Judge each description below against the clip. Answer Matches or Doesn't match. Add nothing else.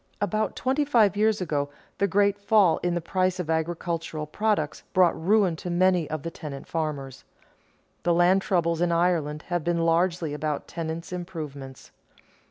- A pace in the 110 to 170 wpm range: Matches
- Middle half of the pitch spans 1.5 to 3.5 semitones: Matches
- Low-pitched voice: Doesn't match